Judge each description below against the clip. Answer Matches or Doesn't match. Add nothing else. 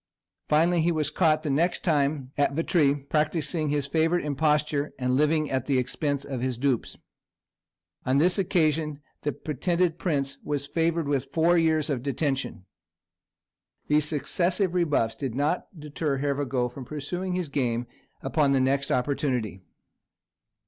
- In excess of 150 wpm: Doesn't match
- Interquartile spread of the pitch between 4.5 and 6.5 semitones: Doesn't match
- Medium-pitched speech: Matches